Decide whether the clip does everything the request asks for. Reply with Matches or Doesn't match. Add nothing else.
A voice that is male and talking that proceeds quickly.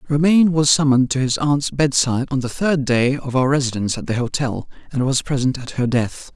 Matches